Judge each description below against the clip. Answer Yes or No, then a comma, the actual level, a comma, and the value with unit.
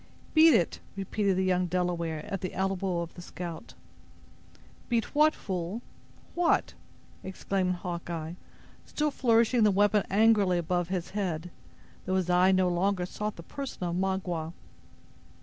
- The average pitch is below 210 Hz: Yes, medium, 185 Hz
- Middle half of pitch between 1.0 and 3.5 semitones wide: Yes, average, 2.8 semitones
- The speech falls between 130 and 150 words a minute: Yes, slow, 135 wpm